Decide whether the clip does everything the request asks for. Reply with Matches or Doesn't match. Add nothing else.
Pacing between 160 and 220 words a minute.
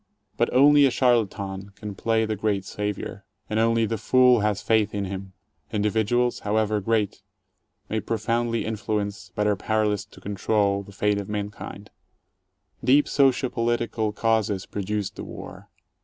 Doesn't match